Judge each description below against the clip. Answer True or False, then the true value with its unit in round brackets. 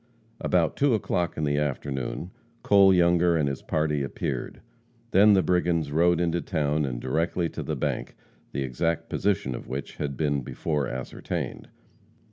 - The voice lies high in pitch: False (80 Hz)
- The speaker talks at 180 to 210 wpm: False (155 wpm)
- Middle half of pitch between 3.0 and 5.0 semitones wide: True (3.8 semitones)